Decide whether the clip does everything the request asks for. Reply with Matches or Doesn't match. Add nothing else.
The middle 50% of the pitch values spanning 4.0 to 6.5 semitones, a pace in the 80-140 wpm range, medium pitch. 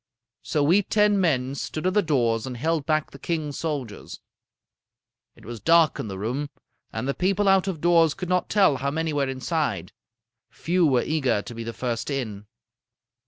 Doesn't match